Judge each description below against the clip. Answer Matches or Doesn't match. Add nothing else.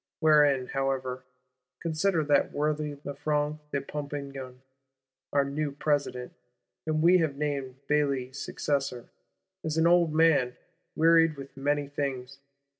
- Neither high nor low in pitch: Matches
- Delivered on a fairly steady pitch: Matches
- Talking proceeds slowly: Matches